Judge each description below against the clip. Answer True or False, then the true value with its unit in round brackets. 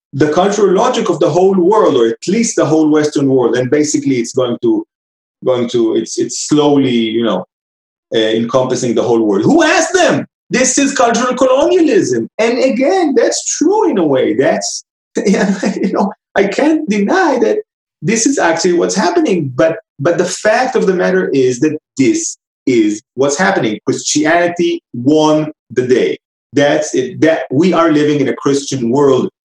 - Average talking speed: True (170 wpm)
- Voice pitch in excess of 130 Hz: True (185 Hz)